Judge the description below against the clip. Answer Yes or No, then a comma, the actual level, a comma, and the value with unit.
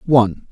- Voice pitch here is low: Yes, low, 120 Hz